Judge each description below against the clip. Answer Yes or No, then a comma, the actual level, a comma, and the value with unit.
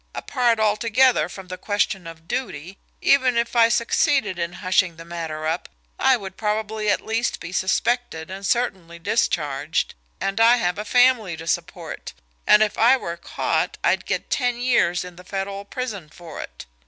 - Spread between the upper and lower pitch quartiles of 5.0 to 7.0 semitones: Yes, average, 5.3 semitones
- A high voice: Yes, high, 200 Hz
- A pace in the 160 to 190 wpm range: Yes, average, 170 wpm